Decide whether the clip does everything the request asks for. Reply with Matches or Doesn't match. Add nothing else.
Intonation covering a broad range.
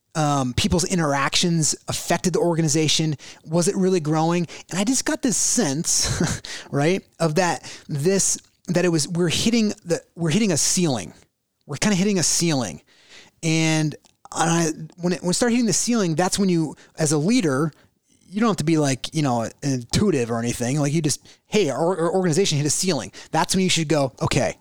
Doesn't match